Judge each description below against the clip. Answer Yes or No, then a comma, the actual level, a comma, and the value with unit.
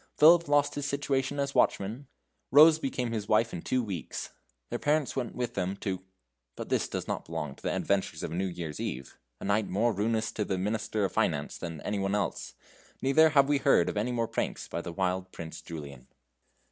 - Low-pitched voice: Yes, low, 110 Hz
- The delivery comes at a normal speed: No, fast, 210 wpm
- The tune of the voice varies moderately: No, wide, 6.6 semitones